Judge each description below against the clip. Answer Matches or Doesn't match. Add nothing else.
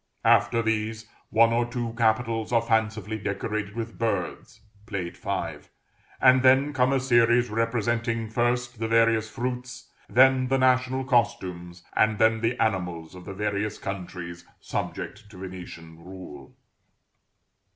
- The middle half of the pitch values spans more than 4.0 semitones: Doesn't match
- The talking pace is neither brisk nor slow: Doesn't match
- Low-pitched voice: Matches